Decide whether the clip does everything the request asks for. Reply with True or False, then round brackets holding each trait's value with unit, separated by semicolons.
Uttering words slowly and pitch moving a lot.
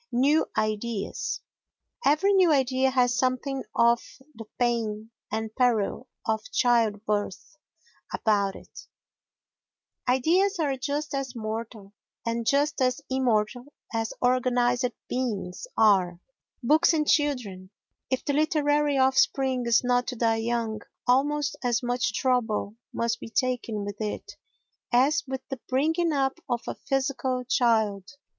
False (125 wpm; 3.4 semitones)